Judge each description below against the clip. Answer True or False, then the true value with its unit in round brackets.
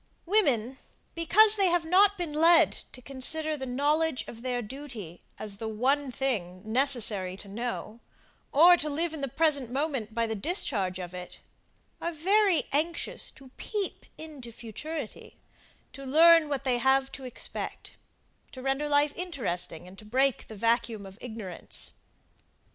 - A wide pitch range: True (6.0 semitones)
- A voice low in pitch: False (270 Hz)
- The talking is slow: False (155 wpm)